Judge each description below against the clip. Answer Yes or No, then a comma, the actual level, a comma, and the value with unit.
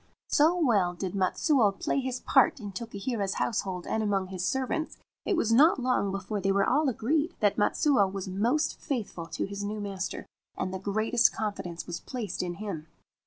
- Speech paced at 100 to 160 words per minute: No, average, 185 wpm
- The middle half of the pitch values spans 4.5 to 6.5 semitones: Yes, average, 4.8 semitones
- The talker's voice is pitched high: Yes, high, 205 Hz